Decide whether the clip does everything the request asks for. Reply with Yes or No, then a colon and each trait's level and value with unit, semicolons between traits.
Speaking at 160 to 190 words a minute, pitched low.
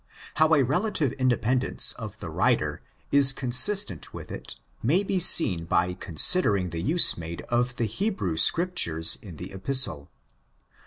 No: average, 145 wpm; low, 125 Hz